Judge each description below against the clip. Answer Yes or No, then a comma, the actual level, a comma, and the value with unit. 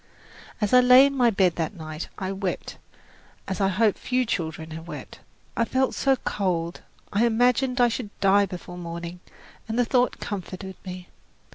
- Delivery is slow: No, average, 170 wpm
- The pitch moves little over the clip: No, wide, 5.5 semitones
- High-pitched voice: Yes, high, 200 Hz